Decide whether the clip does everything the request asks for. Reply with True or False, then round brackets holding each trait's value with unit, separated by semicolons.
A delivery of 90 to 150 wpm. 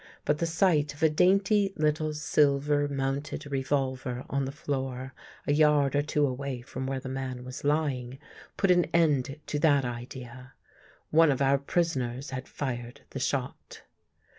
False (160 wpm)